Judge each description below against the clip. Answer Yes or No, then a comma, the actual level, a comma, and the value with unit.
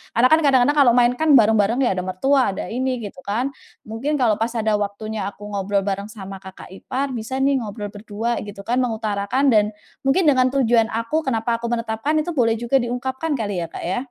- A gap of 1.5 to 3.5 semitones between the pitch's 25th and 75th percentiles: No, average, 3.9 semitones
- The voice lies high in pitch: Yes, high, 230 Hz